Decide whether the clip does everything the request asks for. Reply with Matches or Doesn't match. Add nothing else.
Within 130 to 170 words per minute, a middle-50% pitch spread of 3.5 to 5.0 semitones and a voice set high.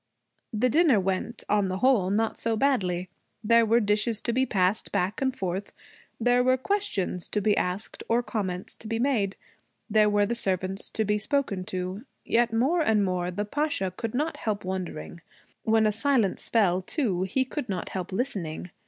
Doesn't match